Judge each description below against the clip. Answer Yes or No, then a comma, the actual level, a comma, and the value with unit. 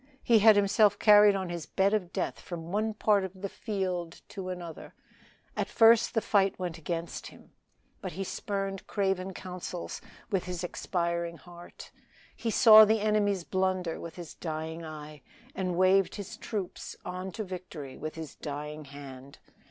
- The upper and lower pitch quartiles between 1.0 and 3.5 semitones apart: Yes, average, 3.1 semitones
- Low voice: No, medium, 185 Hz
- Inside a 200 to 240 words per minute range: No, average, 160 wpm